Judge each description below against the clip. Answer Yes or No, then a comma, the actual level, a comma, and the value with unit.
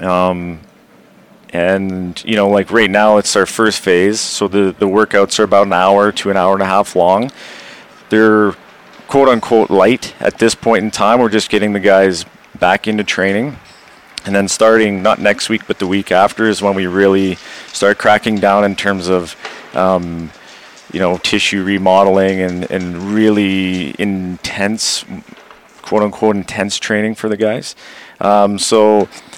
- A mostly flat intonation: Yes, narrow, 2.0 semitones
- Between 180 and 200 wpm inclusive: No, average, 165 wpm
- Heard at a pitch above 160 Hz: No, low, 100 Hz